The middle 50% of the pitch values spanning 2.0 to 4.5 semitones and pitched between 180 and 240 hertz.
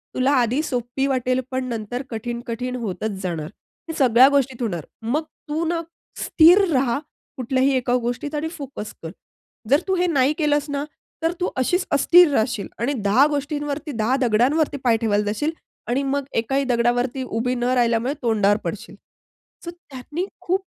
No: average, 3.8 semitones; very high, 255 Hz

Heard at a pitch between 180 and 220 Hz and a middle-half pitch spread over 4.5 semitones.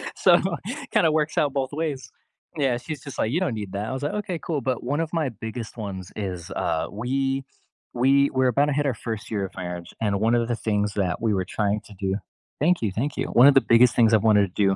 No: low, 120 Hz; average, 5.2 semitones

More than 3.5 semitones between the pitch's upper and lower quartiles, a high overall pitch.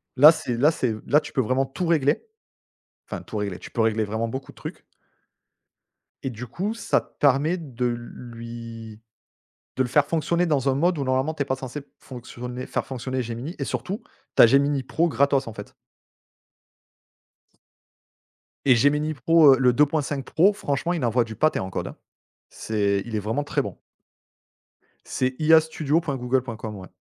No: average, 4.2 semitones; low, 130 Hz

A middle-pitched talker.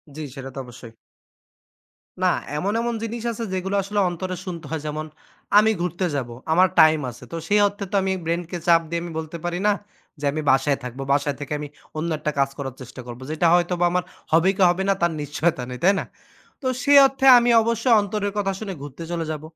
Yes: medium, 170 Hz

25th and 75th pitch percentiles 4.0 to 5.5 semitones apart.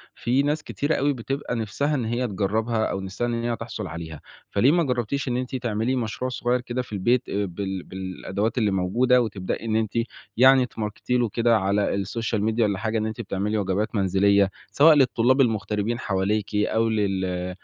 No: average, 3.6 semitones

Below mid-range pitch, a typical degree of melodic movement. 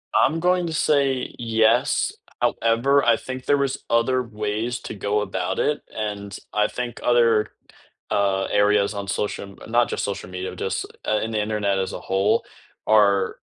Yes: low, 110 Hz; average, 3.2 semitones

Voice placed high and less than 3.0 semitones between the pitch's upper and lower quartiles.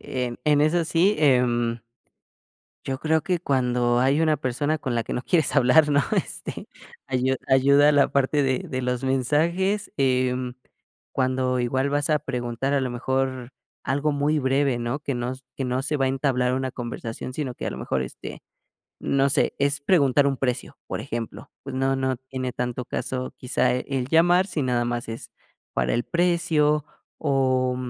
No: low, 130 Hz; narrow, 2.6 semitones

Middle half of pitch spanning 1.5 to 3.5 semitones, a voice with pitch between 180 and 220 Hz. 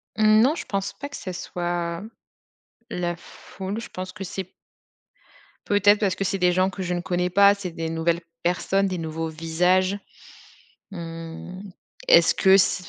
Yes: narrow, 2.4 semitones; medium, 185 Hz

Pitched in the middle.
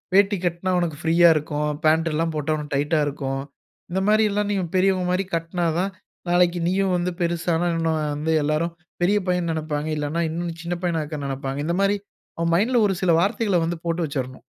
Yes: medium, 170 Hz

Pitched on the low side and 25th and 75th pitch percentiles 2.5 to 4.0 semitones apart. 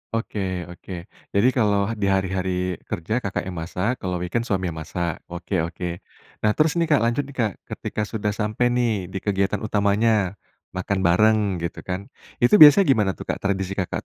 Yes: low, 100 Hz; average, 3.4 semitones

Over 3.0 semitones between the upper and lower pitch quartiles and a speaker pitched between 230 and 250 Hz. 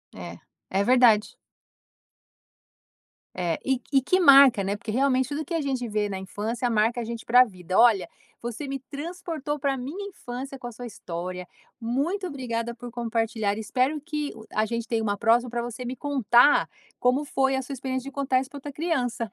Yes: average, 3.6 semitones; high, 245 Hz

